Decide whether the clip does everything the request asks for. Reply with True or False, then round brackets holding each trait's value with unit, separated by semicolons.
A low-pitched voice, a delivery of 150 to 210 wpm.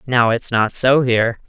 True (125 Hz; 205 wpm)